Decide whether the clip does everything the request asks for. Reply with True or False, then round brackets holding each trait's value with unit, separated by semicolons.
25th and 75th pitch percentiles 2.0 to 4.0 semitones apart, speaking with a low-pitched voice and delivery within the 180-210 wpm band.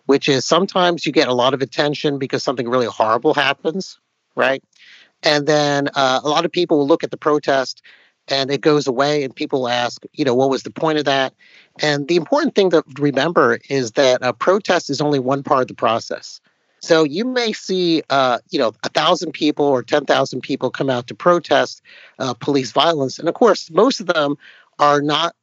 False (3.3 semitones; 145 Hz; 205 wpm)